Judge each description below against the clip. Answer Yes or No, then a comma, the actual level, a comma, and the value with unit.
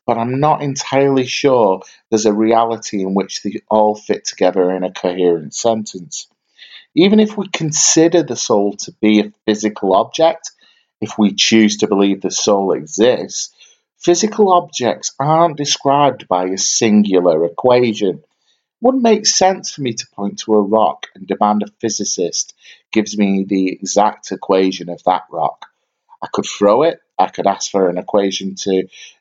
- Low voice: Yes, low, 110 Hz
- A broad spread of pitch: Yes, wide, 7.0 semitones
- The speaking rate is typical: Yes, average, 165 wpm